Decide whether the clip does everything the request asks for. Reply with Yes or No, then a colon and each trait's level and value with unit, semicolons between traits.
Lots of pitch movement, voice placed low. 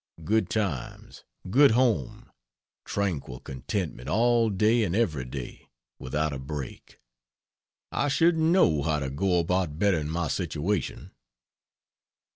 Yes: wide, 7.1 semitones; very low, 90 Hz